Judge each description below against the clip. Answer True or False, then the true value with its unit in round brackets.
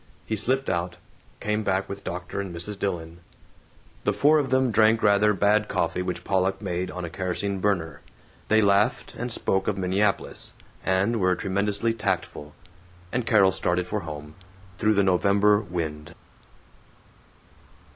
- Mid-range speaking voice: False (100 Hz)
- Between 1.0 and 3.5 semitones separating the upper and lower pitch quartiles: True (2.8 semitones)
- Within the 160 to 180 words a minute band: False (145 wpm)